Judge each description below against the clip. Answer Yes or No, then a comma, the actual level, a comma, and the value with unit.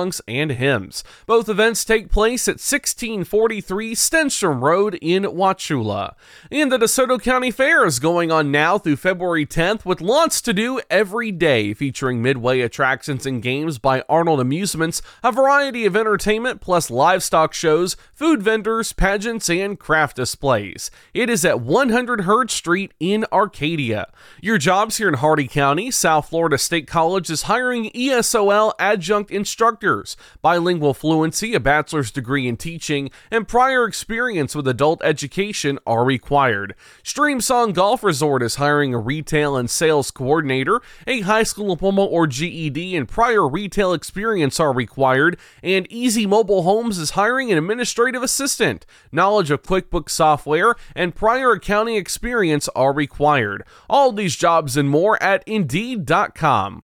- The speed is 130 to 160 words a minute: Yes, average, 145 wpm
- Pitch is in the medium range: Yes, medium, 180 Hz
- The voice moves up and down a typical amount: No, wide, 6.8 semitones